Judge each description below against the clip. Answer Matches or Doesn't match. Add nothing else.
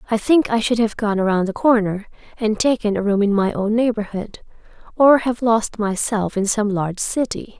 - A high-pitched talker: Matches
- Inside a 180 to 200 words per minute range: Matches